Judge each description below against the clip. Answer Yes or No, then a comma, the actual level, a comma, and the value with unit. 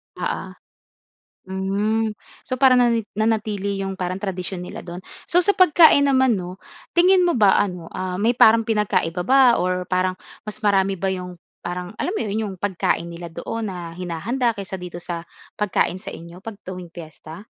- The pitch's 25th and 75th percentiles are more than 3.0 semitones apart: Yes, average, 3.8 semitones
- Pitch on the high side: Yes, high, 195 Hz